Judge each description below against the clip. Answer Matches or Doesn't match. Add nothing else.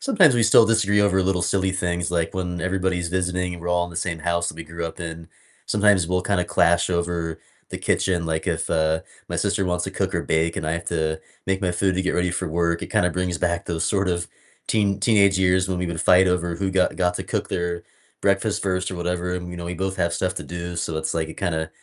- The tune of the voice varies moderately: Doesn't match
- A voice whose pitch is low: Matches